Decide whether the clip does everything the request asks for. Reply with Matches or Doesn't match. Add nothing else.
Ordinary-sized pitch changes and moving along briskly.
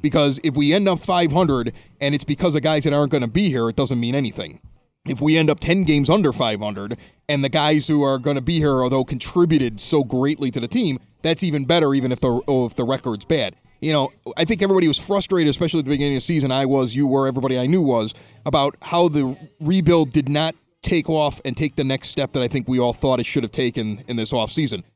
Matches